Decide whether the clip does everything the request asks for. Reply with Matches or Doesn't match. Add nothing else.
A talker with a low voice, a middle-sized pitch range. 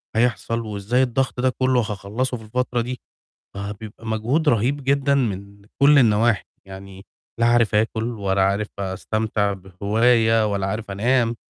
Matches